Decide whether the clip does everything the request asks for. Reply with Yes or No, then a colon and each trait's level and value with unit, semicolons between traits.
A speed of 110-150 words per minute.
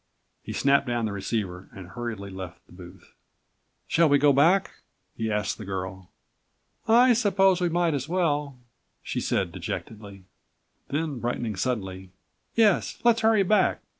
Yes: average, 145 wpm